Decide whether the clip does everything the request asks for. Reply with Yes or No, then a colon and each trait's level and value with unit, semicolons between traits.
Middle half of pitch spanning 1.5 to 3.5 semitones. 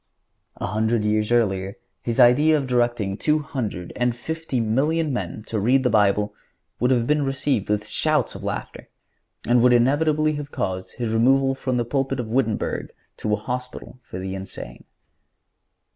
No: average, 4.0 semitones